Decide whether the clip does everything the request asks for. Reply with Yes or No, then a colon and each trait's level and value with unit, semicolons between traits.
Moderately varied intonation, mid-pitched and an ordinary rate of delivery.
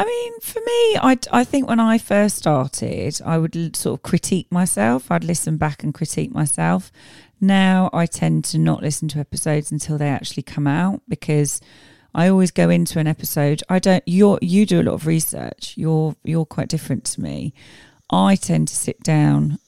Yes: average, 4.0 semitones; medium, 165 Hz; average, 190 wpm